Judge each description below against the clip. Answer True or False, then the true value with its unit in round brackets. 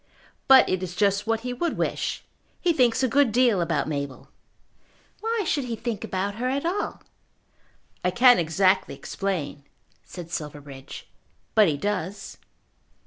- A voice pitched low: False (200 Hz)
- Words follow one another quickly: False (145 wpm)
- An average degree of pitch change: False (6.4 semitones)